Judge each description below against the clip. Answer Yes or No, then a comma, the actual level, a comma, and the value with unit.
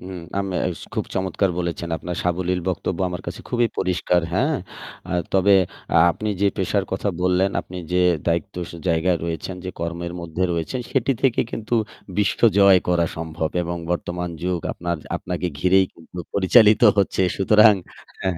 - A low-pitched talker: Yes, very low, 90 Hz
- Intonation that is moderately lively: No, narrow, 2.3 semitones